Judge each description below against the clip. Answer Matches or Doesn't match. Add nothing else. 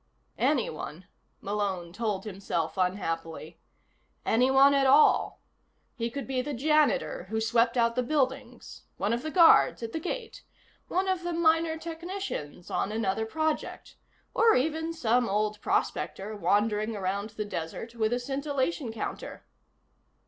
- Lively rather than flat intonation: Matches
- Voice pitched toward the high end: Matches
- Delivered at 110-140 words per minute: Matches